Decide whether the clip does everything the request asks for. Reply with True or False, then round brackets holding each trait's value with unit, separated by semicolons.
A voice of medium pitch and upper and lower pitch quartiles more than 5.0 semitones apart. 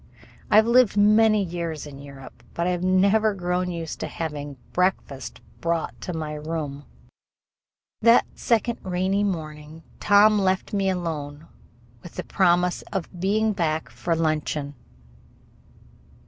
False (175 Hz; 4.4 semitones)